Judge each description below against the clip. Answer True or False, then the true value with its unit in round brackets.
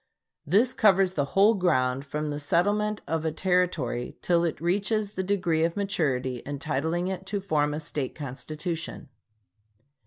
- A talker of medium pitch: True (170 Hz)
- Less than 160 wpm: True (150 wpm)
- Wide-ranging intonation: False (4.5 semitones)